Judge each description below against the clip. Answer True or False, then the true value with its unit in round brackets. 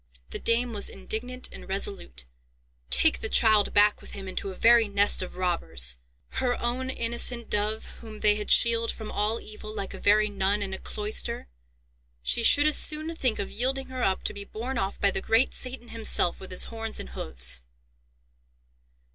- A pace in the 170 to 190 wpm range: True (180 wpm)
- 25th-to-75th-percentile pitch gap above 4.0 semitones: False (3.5 semitones)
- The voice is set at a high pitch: True (215 Hz)